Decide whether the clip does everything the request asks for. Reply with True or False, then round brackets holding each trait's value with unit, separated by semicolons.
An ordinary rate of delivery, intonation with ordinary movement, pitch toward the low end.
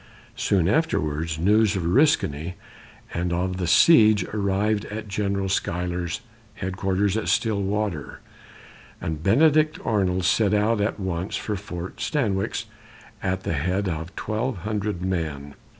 False (125 wpm; 3.3 semitones; 95 Hz)